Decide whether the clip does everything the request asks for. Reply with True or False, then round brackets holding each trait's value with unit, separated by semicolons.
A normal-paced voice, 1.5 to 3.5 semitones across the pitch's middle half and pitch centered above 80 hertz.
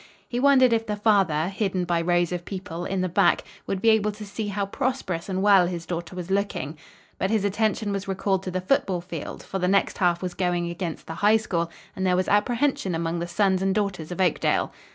False (225 wpm; 2.8 semitones; 190 Hz)